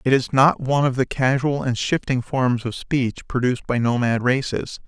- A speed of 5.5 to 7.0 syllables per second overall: No, 5.1 syllables/s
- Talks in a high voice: No, low, 130 Hz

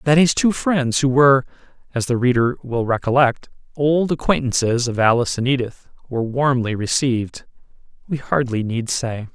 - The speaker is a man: Yes, male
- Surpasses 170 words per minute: No, average, 155 wpm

